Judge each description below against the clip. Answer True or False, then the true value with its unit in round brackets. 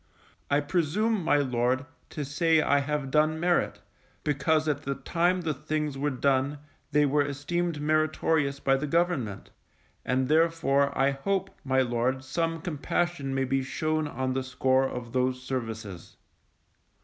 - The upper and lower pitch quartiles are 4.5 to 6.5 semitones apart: False (3.0 semitones)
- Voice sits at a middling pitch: True (145 Hz)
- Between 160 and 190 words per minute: False (150 wpm)